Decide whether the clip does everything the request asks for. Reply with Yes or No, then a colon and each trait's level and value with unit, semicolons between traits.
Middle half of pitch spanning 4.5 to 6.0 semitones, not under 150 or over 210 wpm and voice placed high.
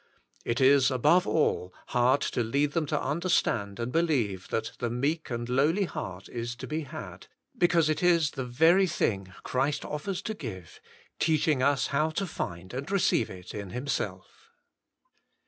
No: wide, 5.4 semitones; average, 165 wpm; medium, 140 Hz